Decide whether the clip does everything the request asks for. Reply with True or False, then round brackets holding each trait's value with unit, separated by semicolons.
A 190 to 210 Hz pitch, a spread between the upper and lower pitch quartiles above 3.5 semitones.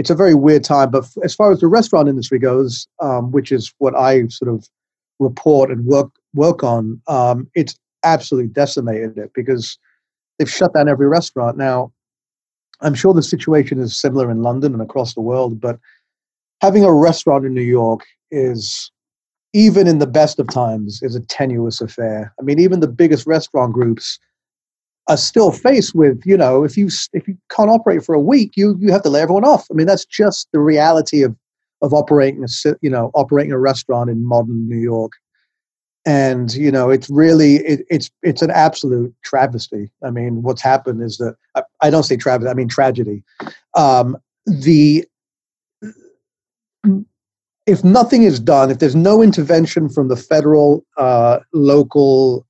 False (140 Hz; 4.6 semitones)